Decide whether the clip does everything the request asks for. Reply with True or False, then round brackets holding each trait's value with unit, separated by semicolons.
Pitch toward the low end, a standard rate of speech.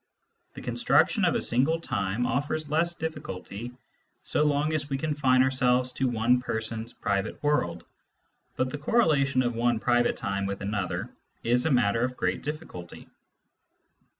True (125 Hz; 150 wpm)